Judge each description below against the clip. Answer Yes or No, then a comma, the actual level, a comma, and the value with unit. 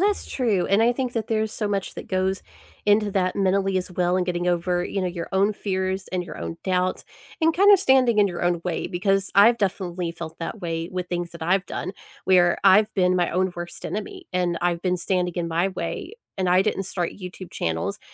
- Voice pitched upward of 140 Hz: Yes, medium, 185 Hz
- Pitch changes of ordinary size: No, narrow, 2.3 semitones